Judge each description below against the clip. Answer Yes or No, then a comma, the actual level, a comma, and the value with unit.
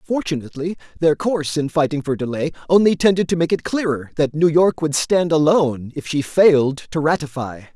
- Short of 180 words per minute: No, average, 185 wpm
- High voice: No, medium, 155 Hz